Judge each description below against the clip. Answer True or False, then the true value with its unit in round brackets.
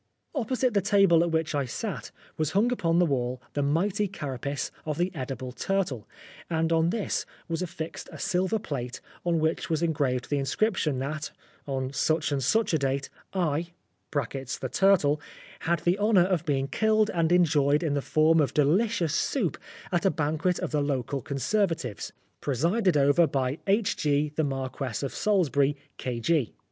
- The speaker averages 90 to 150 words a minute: False (165 wpm)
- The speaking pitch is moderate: True (160 Hz)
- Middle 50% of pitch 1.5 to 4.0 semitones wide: False (4.5 semitones)